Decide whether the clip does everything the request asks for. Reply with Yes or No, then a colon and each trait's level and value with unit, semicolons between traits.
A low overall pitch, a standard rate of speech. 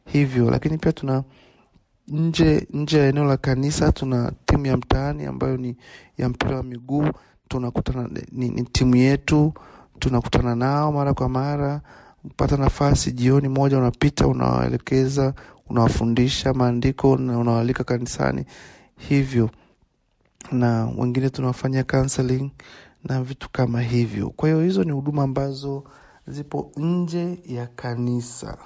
Yes: low, 130 Hz; average, 120 wpm